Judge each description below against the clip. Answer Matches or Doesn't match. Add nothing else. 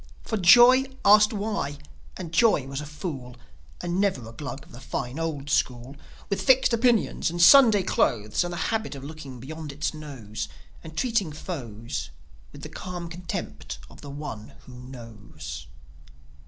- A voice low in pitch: Doesn't match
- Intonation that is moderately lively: Doesn't match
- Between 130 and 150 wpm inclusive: Doesn't match